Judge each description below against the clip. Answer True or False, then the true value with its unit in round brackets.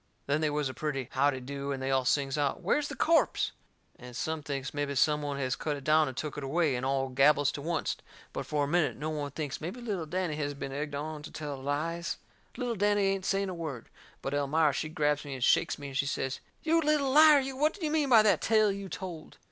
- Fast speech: True (250 wpm)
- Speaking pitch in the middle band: True (150 Hz)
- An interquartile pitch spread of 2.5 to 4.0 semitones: False (5.1 semitones)